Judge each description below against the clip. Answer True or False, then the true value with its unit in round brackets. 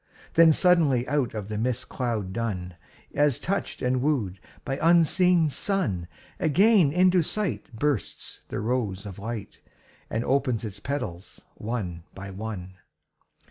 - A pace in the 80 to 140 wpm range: True (135 wpm)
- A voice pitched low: True (125 Hz)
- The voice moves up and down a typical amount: False (7.2 semitones)